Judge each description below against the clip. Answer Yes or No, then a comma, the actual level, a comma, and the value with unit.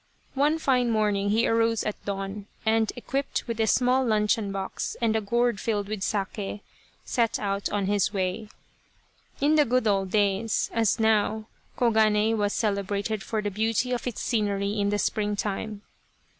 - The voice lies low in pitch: No, high, 215 Hz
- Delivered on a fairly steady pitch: Yes, narrow, 2.1 semitones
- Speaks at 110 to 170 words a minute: Yes, average, 165 wpm